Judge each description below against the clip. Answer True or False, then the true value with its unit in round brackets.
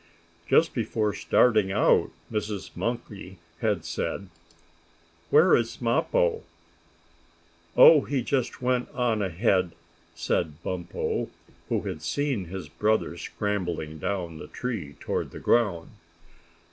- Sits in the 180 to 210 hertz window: False (105 Hz)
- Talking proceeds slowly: True (110 wpm)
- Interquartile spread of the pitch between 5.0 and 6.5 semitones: True (5.5 semitones)